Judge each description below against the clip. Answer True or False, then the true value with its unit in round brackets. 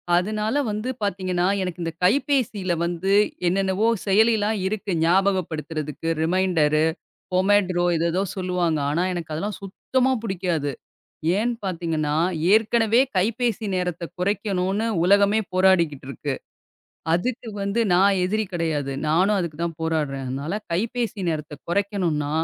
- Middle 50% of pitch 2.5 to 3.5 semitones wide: False (4.0 semitones)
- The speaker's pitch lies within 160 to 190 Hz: True (185 Hz)